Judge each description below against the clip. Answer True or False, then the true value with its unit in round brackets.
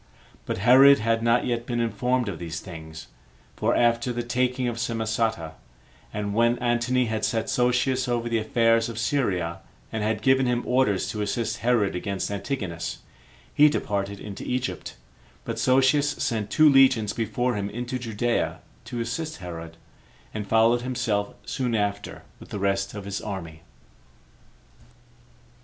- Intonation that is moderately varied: True (3.3 semitones)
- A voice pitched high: False (115 Hz)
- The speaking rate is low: False (150 wpm)